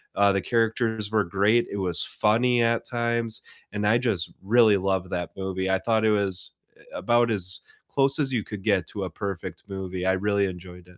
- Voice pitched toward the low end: Yes, low, 100 Hz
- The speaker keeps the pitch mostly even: No, average, 3.4 semitones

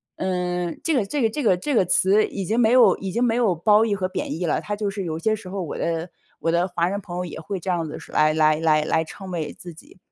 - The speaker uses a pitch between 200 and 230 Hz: No, medium, 185 Hz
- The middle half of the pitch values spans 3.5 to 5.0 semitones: Yes, average, 3.9 semitones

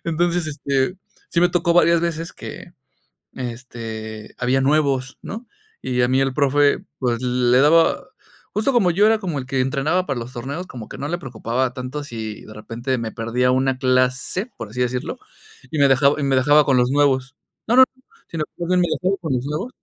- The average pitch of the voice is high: No, low, 135 Hz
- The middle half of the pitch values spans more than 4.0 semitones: Yes, average, 4.7 semitones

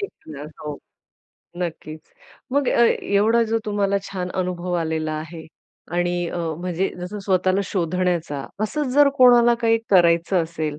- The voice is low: No, medium, 180 Hz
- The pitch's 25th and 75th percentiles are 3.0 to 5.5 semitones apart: Yes, average, 3.9 semitones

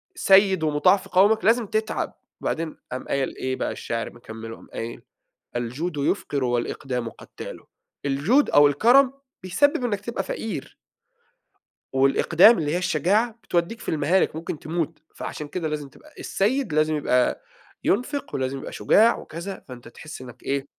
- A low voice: No, medium, 160 Hz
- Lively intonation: Yes, wide, 7.6 semitones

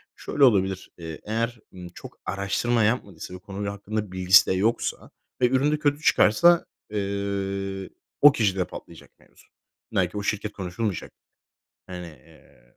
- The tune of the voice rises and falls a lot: No, average, 3.4 semitones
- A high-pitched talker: No, low, 100 Hz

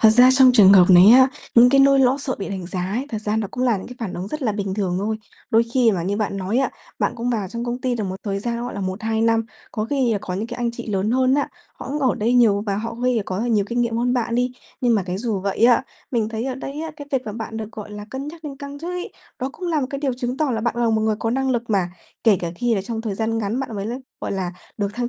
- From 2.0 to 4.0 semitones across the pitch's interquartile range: Yes, average, 3.5 semitones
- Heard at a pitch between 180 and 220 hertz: No, high, 230 Hz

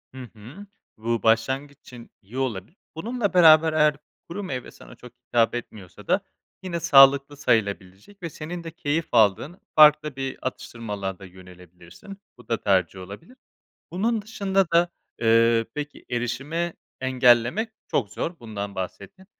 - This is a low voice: Yes, low, 130 Hz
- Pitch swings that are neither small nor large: No, wide, 6.9 semitones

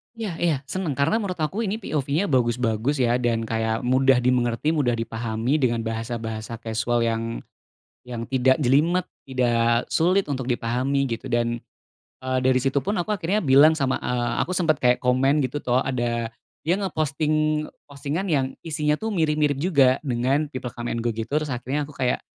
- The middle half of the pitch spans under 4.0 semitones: No, average, 4.3 semitones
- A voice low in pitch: Yes, low, 130 Hz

